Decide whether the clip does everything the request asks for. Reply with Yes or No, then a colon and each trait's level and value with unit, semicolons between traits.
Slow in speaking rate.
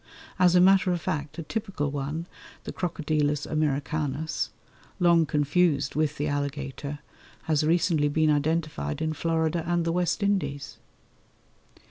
Yes: slow, 130 wpm